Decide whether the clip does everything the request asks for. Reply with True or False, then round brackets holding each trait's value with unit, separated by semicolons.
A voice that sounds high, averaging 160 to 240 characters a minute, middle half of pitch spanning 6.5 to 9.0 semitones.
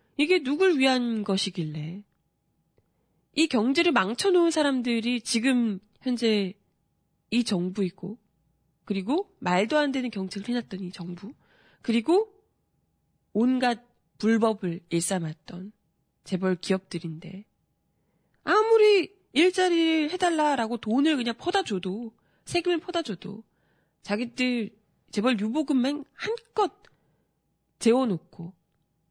True (230 Hz; 225 characters per minute; 7.9 semitones)